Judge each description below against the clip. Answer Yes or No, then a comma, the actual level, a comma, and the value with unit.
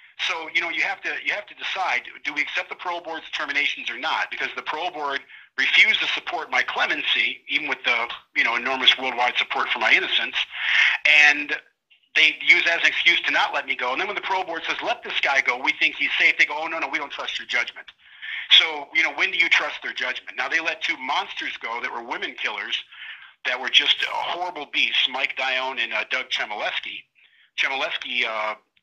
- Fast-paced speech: Yes, fast, 225 wpm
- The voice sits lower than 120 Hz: No, low, 130 Hz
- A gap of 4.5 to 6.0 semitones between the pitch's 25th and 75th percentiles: No, average, 3.3 semitones